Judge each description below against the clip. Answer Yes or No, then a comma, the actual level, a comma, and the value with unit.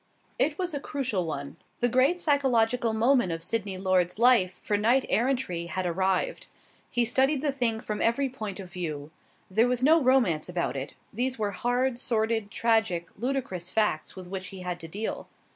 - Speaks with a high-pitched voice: Yes, high, 220 Hz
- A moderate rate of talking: Yes, average, 175 wpm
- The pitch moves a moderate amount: No, wide, 5.7 semitones